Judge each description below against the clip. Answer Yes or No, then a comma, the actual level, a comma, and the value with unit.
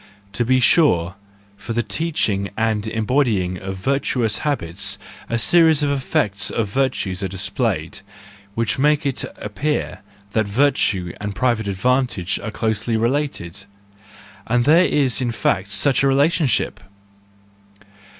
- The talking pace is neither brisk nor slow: No, slow, 130 wpm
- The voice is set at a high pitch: No, low, 115 Hz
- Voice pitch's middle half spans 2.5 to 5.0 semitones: No, wide, 5.4 semitones